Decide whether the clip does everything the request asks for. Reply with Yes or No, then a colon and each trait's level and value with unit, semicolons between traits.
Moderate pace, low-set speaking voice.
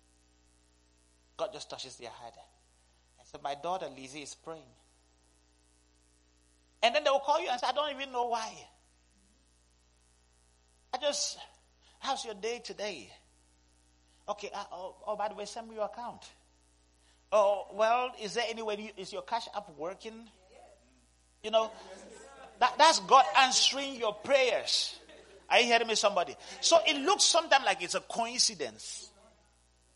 No: average, 150 wpm; medium, 160 Hz